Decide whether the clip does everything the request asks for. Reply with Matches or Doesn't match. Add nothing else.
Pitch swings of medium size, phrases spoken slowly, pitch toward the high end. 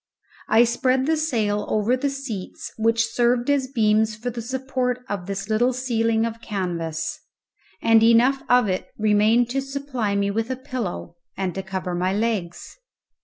Doesn't match